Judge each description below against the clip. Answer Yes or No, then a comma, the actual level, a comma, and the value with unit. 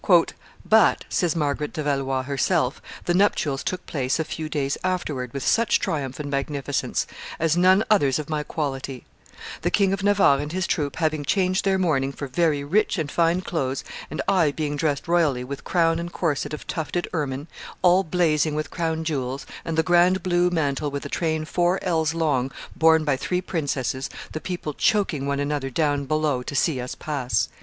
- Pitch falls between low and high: Yes, medium, 155 Hz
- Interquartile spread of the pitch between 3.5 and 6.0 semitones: Yes, average, 3.8 semitones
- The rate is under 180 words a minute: No, average, 185 wpm